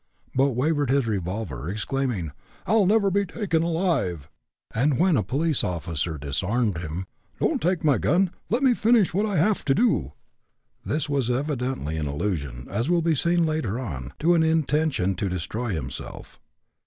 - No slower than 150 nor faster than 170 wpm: Yes, average, 165 wpm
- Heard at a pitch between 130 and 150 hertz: Yes, low, 135 Hz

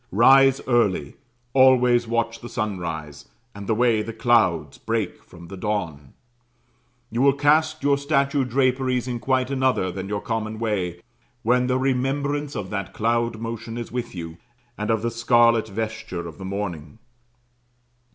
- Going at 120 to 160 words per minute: Yes, average, 150 wpm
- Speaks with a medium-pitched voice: No, low, 115 Hz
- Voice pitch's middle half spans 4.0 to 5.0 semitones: Yes, average, 4.5 semitones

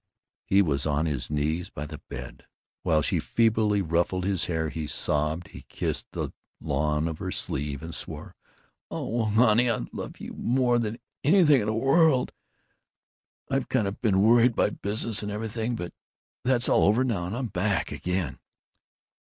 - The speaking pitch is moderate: No, low, 100 Hz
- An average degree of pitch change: No, wide, 6.8 semitones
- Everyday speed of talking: Yes, average, 165 wpm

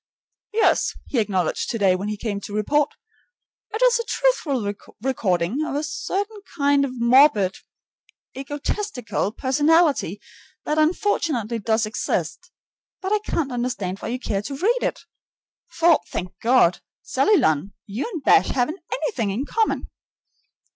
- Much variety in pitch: Yes, wide, 7.5 semitones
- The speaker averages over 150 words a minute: No, average, 140 wpm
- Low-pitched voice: No, very high, 260 Hz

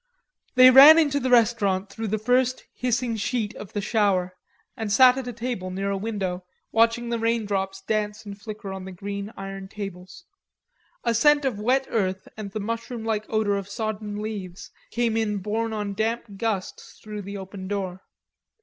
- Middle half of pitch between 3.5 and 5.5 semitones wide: No, average, 2.8 semitones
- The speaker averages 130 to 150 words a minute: No, average, 180 wpm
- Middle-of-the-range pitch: No, high, 215 Hz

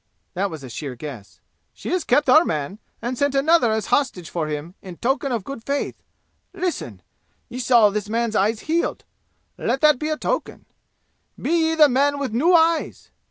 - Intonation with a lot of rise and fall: Yes, wide, 7.3 semitones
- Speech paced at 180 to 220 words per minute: Yes, average, 185 wpm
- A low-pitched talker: No, very high, 250 Hz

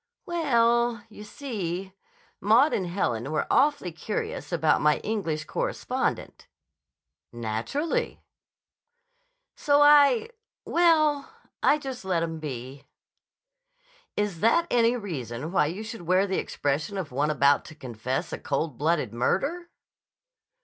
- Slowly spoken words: Yes, slow, 120 wpm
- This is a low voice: No, high, 190 Hz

